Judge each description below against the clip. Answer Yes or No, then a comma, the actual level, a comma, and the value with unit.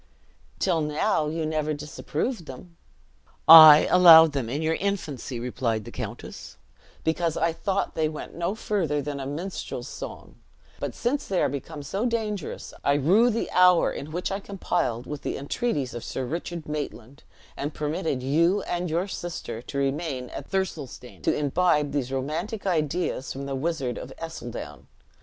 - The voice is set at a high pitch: No, medium, 155 Hz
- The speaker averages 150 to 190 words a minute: Yes, average, 160 wpm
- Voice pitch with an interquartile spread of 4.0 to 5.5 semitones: Yes, average, 4.3 semitones